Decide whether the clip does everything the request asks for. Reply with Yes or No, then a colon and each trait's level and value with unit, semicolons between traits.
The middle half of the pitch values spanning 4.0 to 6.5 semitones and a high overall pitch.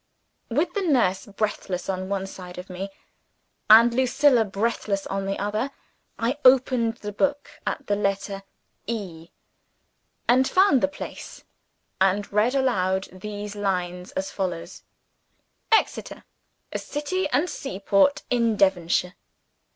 Yes: average, 4.9 semitones; high, 205 Hz